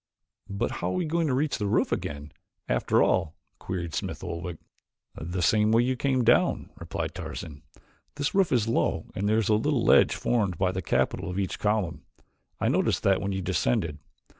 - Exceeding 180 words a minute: Yes, average, 190 wpm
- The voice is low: Yes, low, 100 Hz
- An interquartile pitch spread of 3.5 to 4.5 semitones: No, average, 5.3 semitones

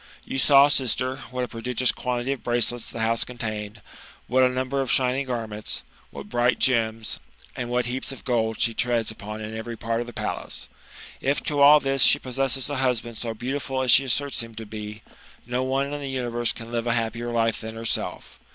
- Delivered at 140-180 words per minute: No, fast, 205 wpm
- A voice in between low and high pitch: No, low, 120 Hz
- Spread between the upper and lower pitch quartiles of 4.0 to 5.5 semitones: No, narrow, 2.4 semitones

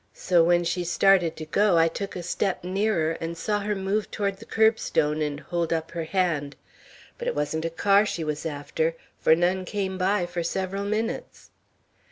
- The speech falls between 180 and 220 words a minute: Yes, average, 190 wpm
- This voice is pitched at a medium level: Yes, medium, 175 Hz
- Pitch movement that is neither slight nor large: Yes, average, 3.4 semitones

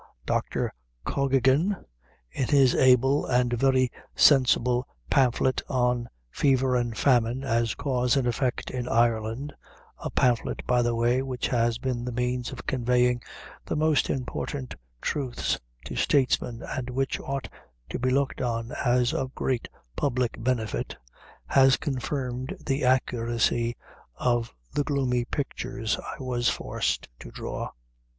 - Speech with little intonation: Yes, narrow, 1.7 semitones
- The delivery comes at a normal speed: No, slow, 130 wpm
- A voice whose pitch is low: Yes, low, 125 Hz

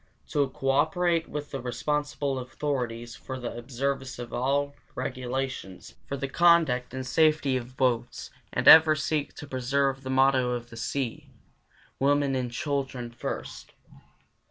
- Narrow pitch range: Yes, narrow, 2.3 semitones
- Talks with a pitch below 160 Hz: Yes, low, 135 Hz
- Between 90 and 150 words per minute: Yes, average, 140 wpm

